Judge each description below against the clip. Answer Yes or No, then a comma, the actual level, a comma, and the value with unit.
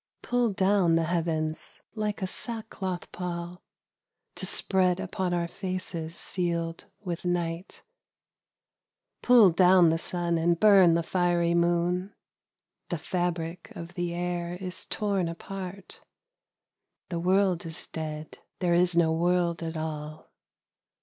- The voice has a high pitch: No, medium, 175 Hz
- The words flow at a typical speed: No, slow, 125 wpm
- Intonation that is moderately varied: No, narrow, 1.8 semitones